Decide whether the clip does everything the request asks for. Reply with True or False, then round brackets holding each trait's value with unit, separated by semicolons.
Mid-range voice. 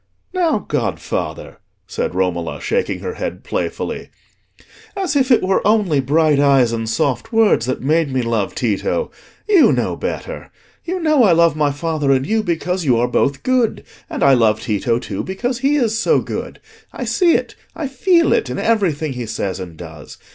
True (160 Hz)